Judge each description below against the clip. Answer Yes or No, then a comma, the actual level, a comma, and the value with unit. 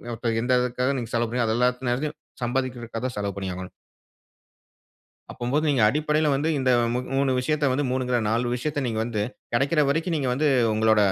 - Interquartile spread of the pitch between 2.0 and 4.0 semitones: Yes, average, 3.4 semitones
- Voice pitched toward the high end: No, low, 125 Hz